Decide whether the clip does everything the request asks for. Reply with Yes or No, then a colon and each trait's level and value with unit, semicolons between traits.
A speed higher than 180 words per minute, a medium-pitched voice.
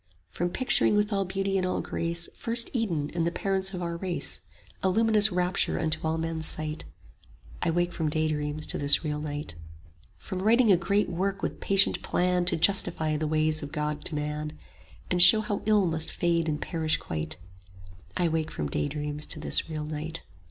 Yes: average, 195 wpm; medium, 165 Hz